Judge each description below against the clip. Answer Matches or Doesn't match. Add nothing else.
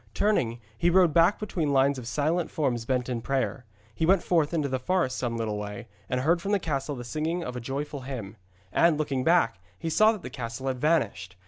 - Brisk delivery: Matches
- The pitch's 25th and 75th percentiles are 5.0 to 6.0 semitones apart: Matches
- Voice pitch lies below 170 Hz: Matches